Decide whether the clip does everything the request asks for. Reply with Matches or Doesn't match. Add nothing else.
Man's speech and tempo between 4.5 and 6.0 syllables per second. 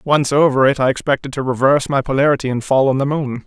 Doesn't match